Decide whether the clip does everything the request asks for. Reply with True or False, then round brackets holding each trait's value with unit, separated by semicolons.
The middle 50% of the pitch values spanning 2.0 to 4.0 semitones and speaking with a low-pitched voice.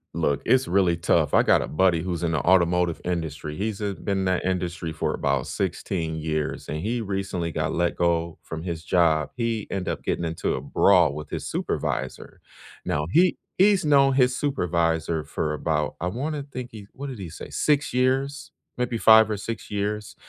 False (5.9 semitones; 90 Hz)